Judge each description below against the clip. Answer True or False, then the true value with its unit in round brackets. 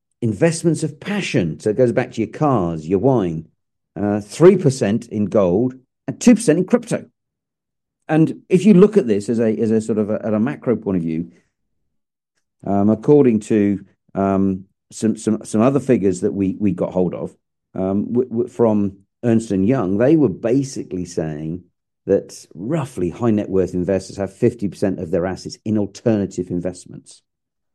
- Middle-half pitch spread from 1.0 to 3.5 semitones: False (4.6 semitones)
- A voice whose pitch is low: True (105 Hz)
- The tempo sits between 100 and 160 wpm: False (175 wpm)